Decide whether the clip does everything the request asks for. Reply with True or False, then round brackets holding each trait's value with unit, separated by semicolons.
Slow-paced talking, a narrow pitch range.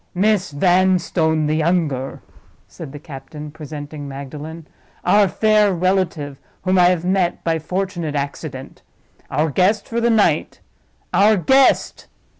False (125 wpm; 4.2 semitones)